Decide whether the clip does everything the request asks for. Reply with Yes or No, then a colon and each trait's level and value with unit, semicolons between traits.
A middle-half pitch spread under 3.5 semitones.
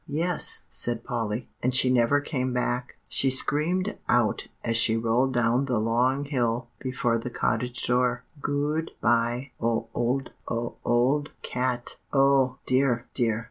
Yes: narrow, 2.4 semitones